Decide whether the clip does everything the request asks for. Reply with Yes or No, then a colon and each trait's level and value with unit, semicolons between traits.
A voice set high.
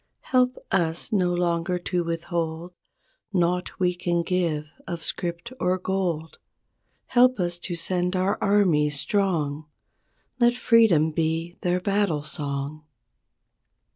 No: medium, 175 Hz